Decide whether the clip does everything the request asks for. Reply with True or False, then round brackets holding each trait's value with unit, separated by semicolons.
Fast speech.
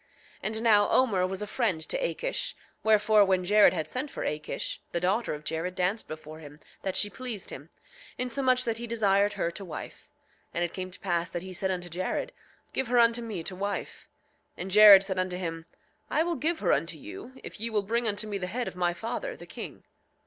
True (220 wpm)